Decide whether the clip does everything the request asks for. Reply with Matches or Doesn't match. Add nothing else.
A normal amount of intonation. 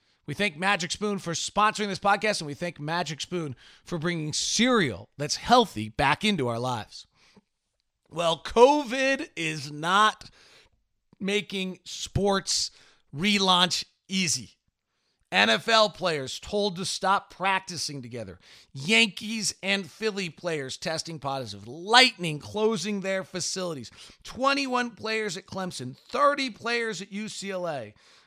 Doesn't match